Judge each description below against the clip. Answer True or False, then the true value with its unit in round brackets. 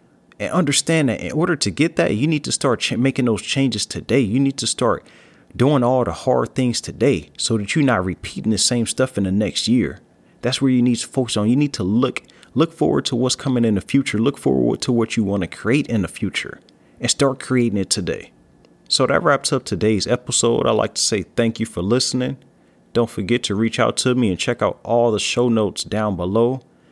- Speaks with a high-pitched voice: False (120 Hz)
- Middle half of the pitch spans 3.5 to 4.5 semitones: True (3.9 semitones)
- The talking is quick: True (230 wpm)